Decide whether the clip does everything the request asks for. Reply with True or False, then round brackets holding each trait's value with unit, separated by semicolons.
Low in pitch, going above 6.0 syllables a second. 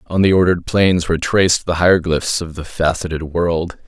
False (85 Hz; 5.4 syllables/s)